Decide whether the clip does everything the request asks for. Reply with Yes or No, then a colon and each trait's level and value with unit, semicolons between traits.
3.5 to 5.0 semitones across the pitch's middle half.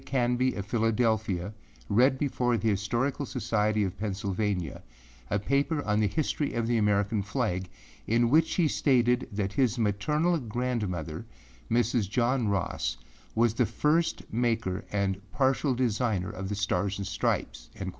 Yes: average, 3.9 semitones